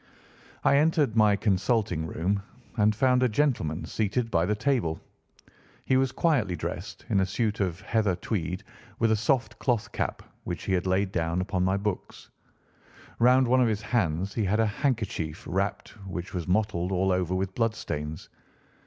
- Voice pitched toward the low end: Yes, low, 100 Hz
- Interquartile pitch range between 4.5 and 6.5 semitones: No, average, 4.1 semitones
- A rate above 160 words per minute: Yes, average, 170 wpm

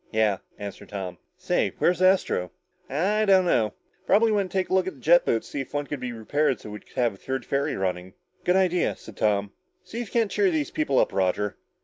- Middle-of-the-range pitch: Yes, medium, 145 Hz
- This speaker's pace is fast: Yes, fast, 235 wpm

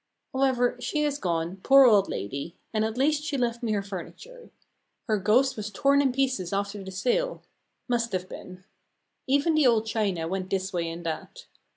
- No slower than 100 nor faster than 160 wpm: No, average, 185 wpm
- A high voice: Yes, high, 220 Hz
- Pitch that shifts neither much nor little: No, wide, 6.2 semitones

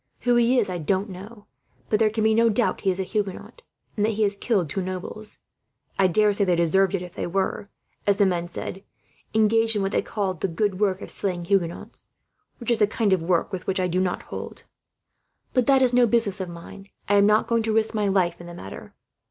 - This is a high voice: Yes, high, 200 Hz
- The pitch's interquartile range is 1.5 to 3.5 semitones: Yes, average, 3.0 semitones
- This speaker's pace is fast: Yes, fast, 235 wpm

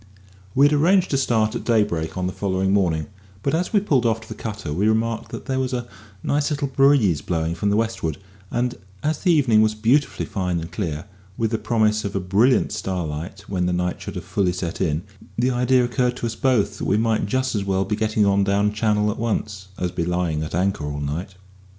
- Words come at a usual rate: No, fast, 225 wpm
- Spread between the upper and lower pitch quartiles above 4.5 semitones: Yes, average, 5.1 semitones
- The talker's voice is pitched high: No, low, 105 Hz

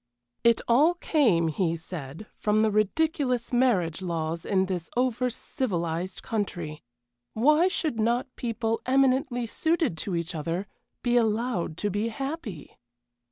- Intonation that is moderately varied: No, wide, 6.6 semitones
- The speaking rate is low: Yes, slow, 130 wpm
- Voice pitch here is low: No, high, 220 Hz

